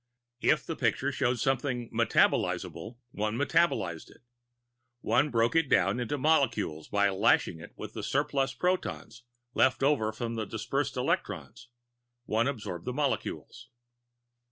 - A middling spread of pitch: Yes, average, 4.4 semitones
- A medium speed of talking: No, slow, 130 wpm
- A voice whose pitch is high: No, low, 120 Hz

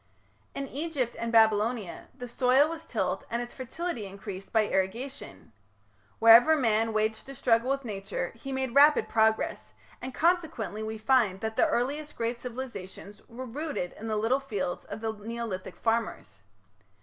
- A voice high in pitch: Yes, high, 230 Hz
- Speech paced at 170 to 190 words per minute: No, average, 155 wpm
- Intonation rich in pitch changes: No, average, 3.4 semitones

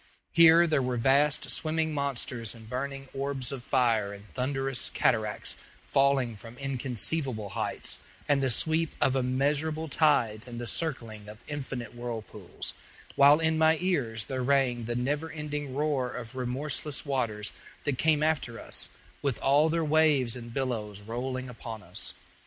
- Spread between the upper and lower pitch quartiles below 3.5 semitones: No, average, 3.8 semitones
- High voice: No, low, 135 Hz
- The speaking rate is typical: Yes, average, 150 wpm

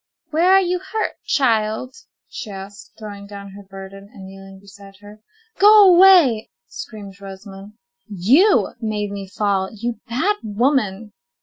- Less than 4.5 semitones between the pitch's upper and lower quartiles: No, average, 5.0 semitones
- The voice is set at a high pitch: Yes, high, 210 Hz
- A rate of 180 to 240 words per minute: No, slow, 135 wpm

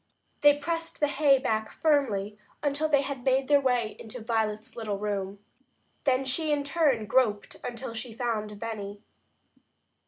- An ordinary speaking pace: Yes, average, 155 wpm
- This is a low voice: No, high, 245 Hz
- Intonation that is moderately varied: Yes, average, 4.8 semitones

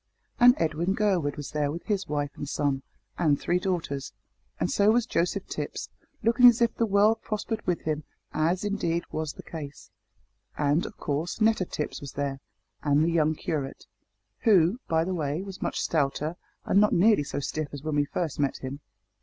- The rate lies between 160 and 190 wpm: Yes, average, 185 wpm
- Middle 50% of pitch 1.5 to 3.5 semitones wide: No, wide, 5.4 semitones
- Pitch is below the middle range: No, medium, 165 Hz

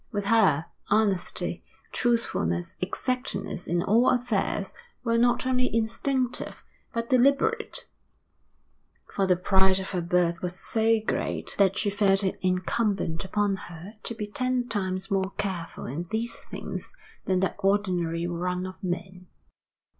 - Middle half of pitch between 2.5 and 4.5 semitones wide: Yes, average, 4.1 semitones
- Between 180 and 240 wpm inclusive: No, slow, 135 wpm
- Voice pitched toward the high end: Yes, high, 195 Hz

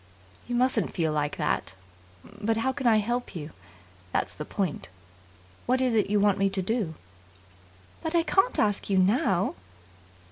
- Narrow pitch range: No, average, 4.9 semitones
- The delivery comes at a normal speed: Yes, average, 155 wpm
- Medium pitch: No, high, 210 Hz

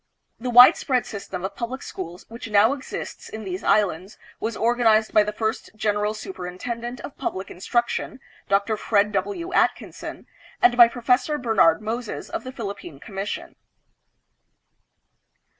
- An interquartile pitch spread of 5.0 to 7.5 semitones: No, average, 3.3 semitones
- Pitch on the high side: Yes, high, 220 Hz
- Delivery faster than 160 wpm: No, average, 140 wpm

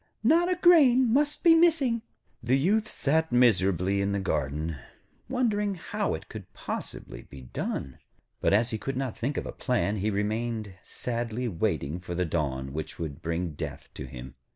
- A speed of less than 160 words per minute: No, average, 175 wpm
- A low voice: Yes, low, 110 Hz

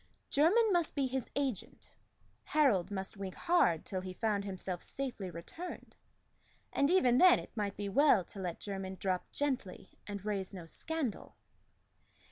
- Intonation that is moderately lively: No, wide, 7.0 semitones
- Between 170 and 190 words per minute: No, average, 150 wpm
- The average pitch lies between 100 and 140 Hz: No, high, 205 Hz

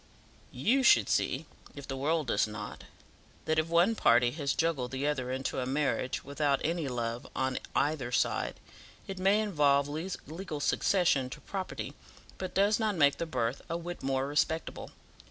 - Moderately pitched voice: Yes, medium, 145 Hz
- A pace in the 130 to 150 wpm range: No, average, 165 wpm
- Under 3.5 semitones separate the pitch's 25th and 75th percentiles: No, average, 4.4 semitones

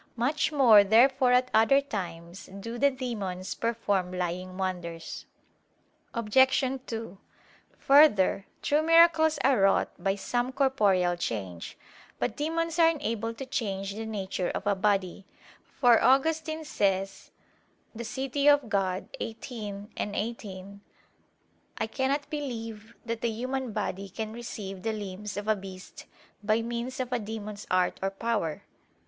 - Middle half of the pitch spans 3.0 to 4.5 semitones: No, average, 5.0 semitones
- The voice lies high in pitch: Yes, high, 220 Hz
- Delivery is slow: Yes, slow, 130 wpm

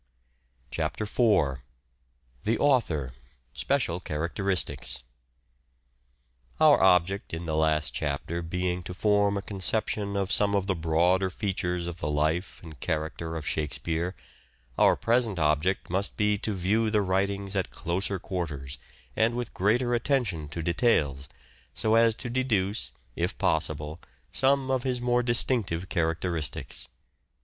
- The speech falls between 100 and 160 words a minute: Yes, average, 140 wpm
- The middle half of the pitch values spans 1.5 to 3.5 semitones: No, average, 5.0 semitones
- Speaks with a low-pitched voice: Yes, very low, 95 Hz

